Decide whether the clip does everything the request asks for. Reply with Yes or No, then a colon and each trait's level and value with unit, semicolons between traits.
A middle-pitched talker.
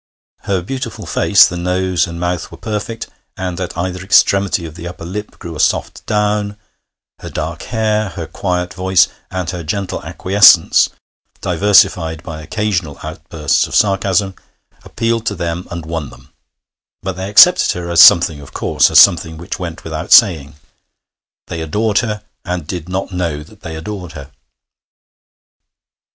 No: very low, 90 Hz